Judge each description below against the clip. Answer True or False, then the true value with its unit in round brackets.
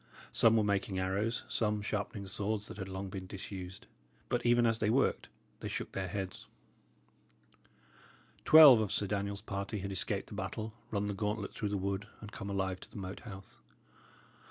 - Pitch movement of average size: False (1.9 semitones)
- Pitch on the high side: False (100 Hz)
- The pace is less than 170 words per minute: False (180 wpm)